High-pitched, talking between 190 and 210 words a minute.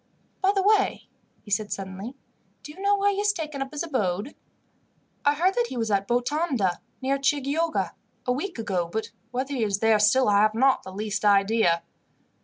Yes: very high, 250 Hz; average, 195 wpm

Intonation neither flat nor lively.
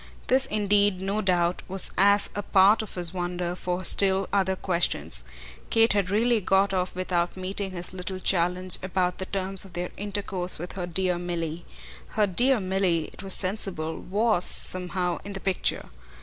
No: narrow, 2.0 semitones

